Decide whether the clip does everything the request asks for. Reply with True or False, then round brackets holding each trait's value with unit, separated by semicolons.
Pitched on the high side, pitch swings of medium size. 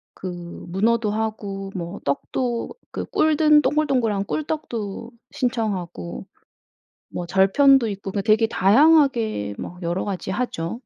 True (215 Hz; 4.9 semitones)